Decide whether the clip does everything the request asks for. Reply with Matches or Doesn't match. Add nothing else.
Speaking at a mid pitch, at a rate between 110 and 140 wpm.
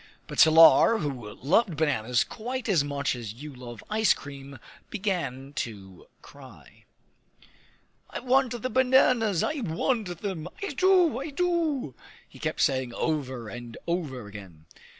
Matches